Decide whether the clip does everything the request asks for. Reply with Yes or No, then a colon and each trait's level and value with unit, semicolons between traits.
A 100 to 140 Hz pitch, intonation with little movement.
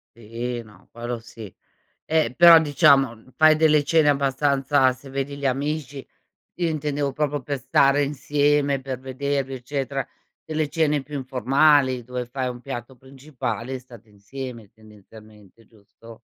No: low, 135 Hz; average, 3.2 semitones